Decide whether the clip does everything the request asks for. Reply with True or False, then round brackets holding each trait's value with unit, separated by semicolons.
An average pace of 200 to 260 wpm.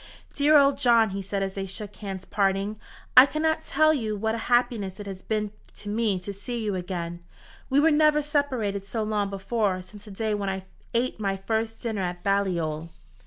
True (205 wpm)